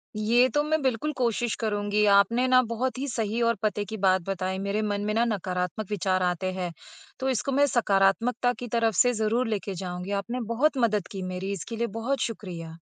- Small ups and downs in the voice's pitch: No, average, 3.9 semitones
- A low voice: No, high, 215 Hz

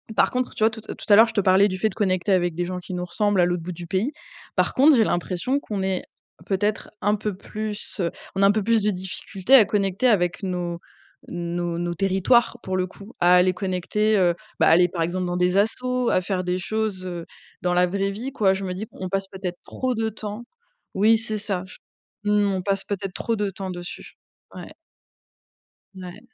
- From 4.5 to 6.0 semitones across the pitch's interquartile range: No, average, 2.9 semitones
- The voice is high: Yes, high, 195 Hz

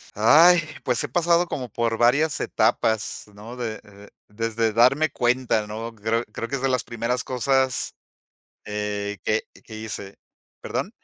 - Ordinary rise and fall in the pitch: Yes, average, 3.1 semitones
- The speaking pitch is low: Yes, low, 115 Hz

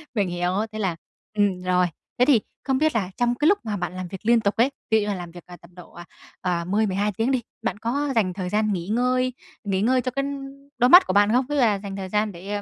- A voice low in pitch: No, high, 210 Hz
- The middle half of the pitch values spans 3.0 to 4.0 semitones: No, average, 4.7 semitones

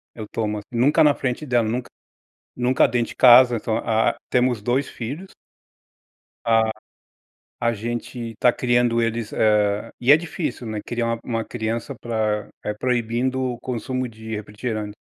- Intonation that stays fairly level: Yes, narrow, 2.1 semitones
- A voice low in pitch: Yes, low, 120 Hz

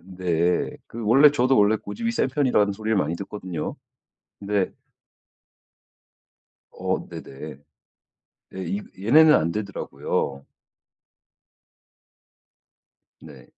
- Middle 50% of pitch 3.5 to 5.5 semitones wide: Yes, average, 5.2 semitones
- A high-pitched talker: No, low, 100 Hz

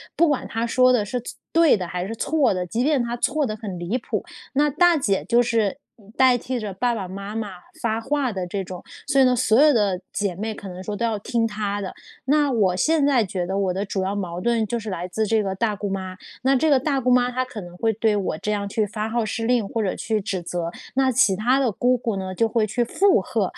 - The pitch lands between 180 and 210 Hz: No, high, 220 Hz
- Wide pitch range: No, average, 4.3 semitones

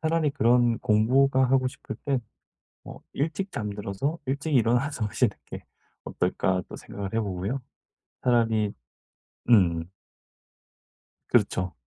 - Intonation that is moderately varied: Yes, average, 5.0 semitones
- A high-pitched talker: No, low, 120 Hz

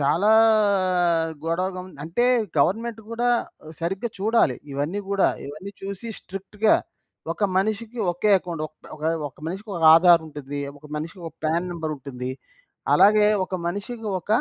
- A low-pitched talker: No, medium, 185 Hz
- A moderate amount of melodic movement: Yes, average, 4.5 semitones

